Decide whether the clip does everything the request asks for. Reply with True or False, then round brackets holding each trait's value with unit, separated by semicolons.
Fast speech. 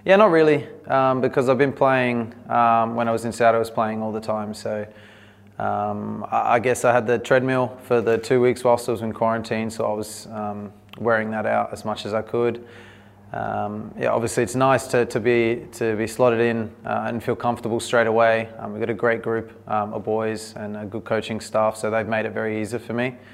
True (230 wpm)